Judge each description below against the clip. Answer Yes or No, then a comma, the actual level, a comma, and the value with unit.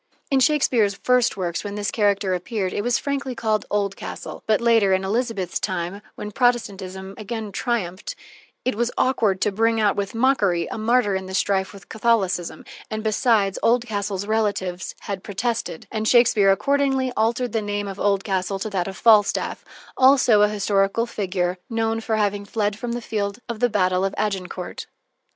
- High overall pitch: Yes, high, 210 Hz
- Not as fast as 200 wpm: Yes, average, 165 wpm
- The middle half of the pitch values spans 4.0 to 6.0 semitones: No, average, 3.0 semitones